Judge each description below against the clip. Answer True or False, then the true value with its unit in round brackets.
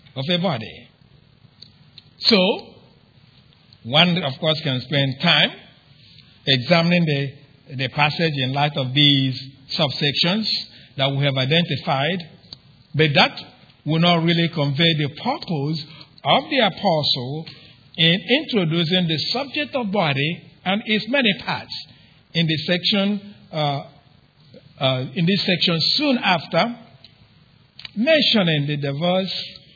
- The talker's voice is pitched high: False (155 Hz)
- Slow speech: True (115 wpm)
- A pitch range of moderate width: True (4.2 semitones)